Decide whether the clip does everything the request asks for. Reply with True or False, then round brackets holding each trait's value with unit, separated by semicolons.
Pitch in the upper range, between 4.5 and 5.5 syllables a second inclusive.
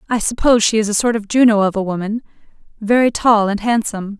False (215 Hz; 6.5 syllables/s)